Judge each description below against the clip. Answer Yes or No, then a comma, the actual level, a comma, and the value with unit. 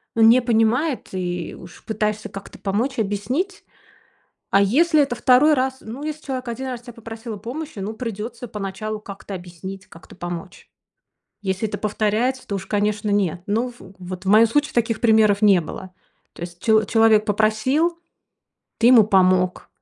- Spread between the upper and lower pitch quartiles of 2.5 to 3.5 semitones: No, average, 3.9 semitones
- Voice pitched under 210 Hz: No, high, 215 Hz